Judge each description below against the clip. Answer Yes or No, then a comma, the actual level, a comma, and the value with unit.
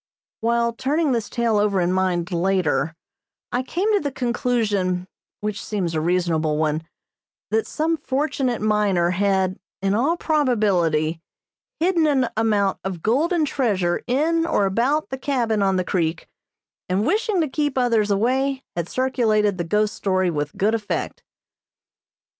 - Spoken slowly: No, average, 145 wpm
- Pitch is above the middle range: Yes, high, 215 Hz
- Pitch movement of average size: No, wide, 6.2 semitones